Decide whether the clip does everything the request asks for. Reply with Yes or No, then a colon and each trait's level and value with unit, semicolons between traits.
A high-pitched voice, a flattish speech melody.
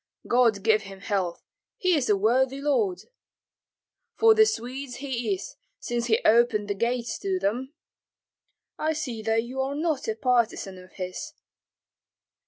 No: high, 240 Hz; average, 4.3 semitones